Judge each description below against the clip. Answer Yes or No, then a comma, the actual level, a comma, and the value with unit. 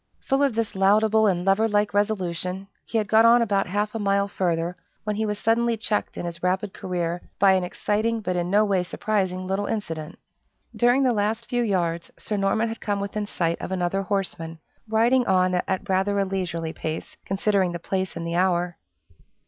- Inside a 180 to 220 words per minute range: Yes, average, 195 wpm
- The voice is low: No, high, 195 Hz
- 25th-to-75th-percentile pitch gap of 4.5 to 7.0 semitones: No, average, 3.0 semitones